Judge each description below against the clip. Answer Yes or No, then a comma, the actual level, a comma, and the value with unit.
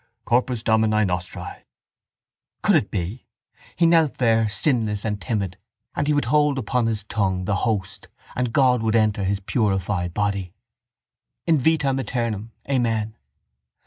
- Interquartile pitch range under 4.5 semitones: Yes, average, 3.9 semitones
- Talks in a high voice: No, low, 110 Hz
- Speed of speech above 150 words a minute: No, average, 140 wpm